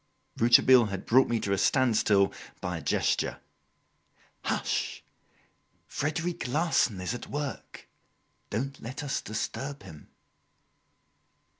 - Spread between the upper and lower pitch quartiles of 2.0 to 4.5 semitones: No, average, 5.1 semitones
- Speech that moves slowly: Yes, slow, 110 wpm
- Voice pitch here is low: Yes, low, 120 Hz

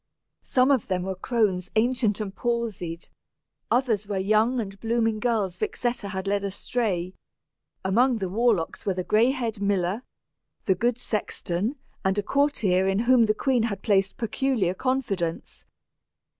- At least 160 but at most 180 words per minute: No, average, 145 wpm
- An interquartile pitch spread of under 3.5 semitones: No, average, 3.8 semitones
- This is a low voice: No, high, 215 Hz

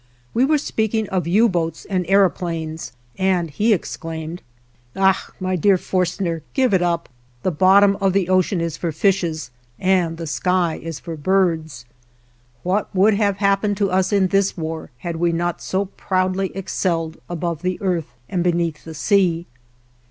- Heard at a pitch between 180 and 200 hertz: Yes, medium, 185 Hz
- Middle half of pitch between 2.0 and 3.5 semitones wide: Yes, average, 2.8 semitones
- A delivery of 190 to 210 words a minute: No, average, 160 wpm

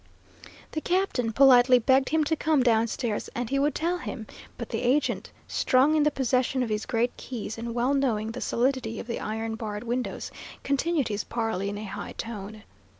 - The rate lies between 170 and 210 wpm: Yes, average, 190 wpm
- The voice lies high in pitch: Yes, high, 245 Hz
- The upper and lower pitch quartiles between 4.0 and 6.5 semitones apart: No, average, 3.6 semitones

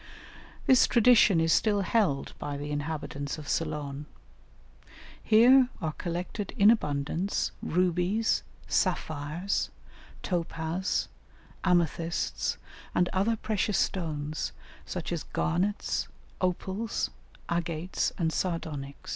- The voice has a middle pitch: Yes, medium, 175 Hz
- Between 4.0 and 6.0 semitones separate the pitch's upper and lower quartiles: Yes, average, 4.5 semitones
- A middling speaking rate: No, slow, 95 wpm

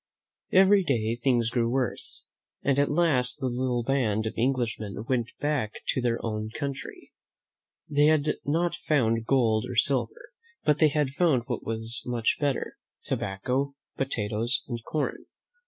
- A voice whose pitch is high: No, low, 130 Hz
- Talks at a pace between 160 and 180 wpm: No, average, 145 wpm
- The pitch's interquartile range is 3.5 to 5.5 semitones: Yes, average, 3.8 semitones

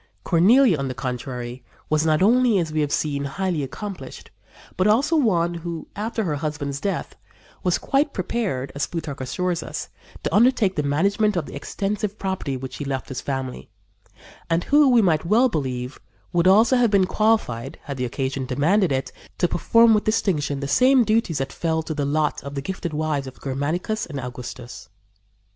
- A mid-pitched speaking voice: Yes, medium, 165 Hz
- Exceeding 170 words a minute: Yes, average, 180 wpm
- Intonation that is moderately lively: No, wide, 7.0 semitones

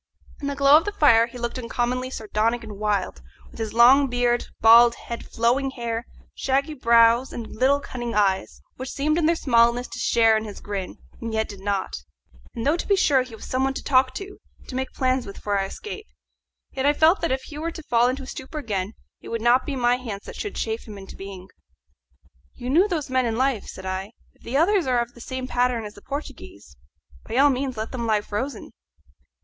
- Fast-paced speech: Yes, fast, 225 wpm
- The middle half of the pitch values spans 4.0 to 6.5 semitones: No, average, 3.4 semitones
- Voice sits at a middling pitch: No, high, 245 Hz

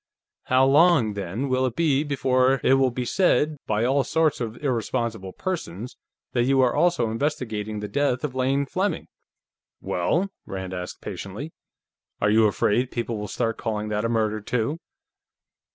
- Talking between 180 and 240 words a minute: No, average, 160 wpm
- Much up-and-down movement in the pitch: No, average, 4.5 semitones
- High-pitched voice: No, low, 125 Hz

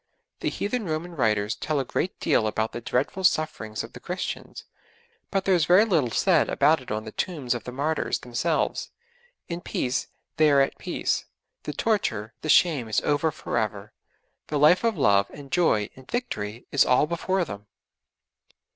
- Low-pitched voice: No, medium, 145 Hz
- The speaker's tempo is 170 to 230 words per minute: Yes, average, 180 wpm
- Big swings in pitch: Yes, wide, 7.3 semitones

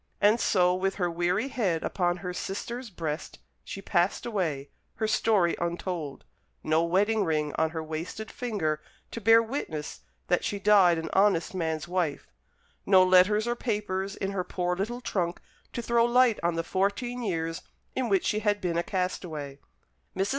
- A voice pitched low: No, medium, 185 Hz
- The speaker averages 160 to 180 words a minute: Yes, average, 170 wpm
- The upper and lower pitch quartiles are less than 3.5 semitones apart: No, average, 3.8 semitones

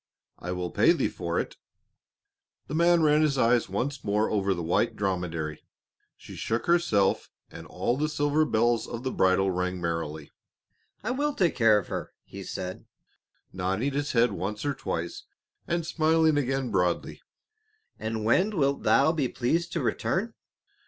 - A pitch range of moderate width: No, wide, 8.2 semitones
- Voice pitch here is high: No, low, 120 Hz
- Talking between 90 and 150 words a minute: No, average, 160 wpm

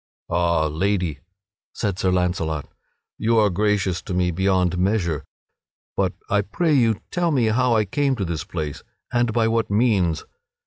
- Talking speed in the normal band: Yes, average, 160 wpm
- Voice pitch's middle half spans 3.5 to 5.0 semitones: Yes, average, 4.3 semitones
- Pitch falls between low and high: No, low, 100 Hz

